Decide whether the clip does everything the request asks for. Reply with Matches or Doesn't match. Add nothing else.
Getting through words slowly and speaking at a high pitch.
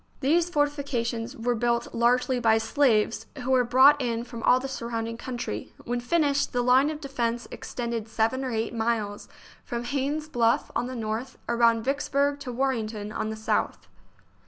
Doesn't match